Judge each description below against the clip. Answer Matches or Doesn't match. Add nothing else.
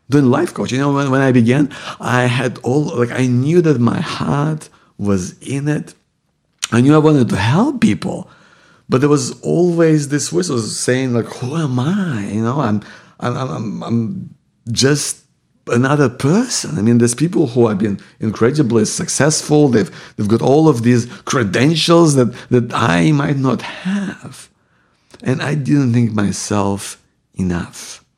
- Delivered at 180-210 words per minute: Doesn't match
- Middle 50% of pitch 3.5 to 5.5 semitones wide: Matches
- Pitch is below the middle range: Matches